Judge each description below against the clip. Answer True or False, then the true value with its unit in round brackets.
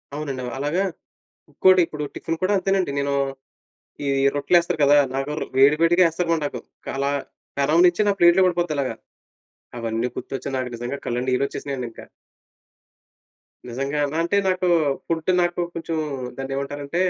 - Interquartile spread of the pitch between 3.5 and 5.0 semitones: True (4.0 semitones)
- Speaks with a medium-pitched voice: True (150 Hz)